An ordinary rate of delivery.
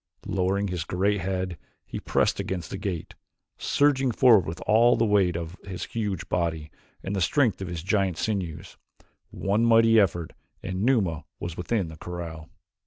Yes: average, 165 wpm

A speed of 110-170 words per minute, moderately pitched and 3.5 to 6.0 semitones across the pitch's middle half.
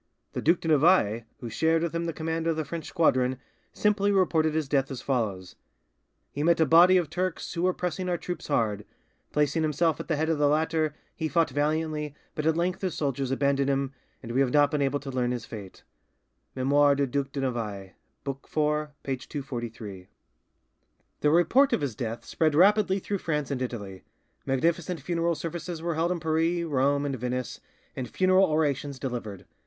No: average, 190 wpm; medium, 150 Hz; average, 3.9 semitones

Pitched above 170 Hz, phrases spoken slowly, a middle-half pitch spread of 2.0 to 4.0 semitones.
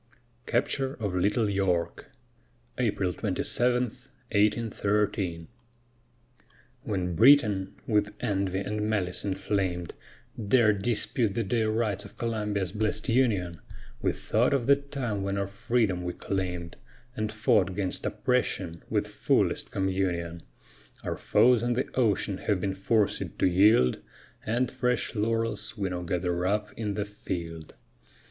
No: low, 105 Hz; slow, 125 wpm; average, 3.4 semitones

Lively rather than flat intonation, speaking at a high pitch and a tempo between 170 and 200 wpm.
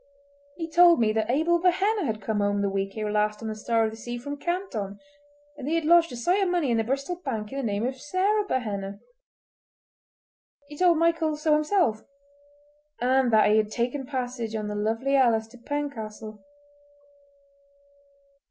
Yes: wide, 6.2 semitones; very high, 260 Hz; average, 180 wpm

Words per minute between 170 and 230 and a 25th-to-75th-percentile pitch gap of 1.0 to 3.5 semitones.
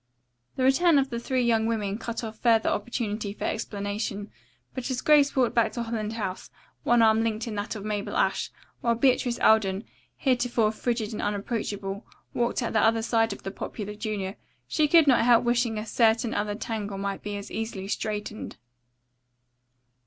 Yes: average, 175 wpm; narrow, 2.4 semitones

